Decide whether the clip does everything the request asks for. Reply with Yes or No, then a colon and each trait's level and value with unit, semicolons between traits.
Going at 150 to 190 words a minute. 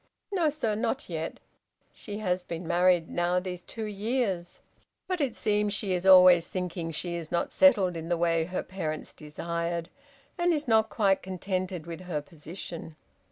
Yes: average, 165 wpm